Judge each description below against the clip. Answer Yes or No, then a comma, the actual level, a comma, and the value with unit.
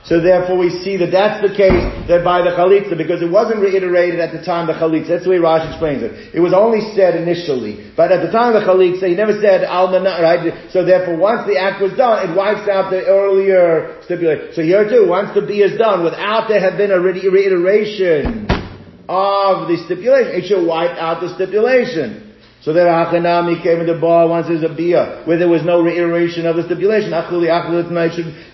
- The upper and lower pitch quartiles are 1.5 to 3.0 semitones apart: Yes, narrow, 2.6 semitones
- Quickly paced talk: Yes, fast, 220 wpm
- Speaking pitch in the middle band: Yes, medium, 180 Hz